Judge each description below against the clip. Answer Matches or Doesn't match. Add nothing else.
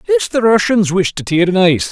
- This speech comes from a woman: Doesn't match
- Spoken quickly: Doesn't match